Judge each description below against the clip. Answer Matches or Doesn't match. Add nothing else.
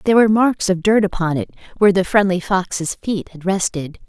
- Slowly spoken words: Doesn't match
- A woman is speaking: Matches